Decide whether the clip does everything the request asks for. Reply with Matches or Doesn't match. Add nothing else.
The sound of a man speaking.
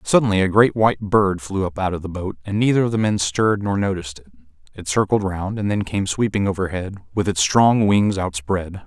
Matches